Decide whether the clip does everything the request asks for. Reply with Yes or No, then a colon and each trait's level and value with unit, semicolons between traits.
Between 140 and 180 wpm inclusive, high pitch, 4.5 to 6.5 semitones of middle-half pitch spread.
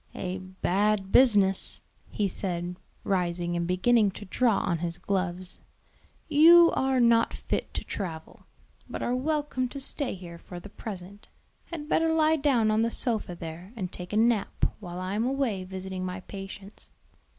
Yes: average, 160 wpm; high, 200 Hz; average, 5.0 semitones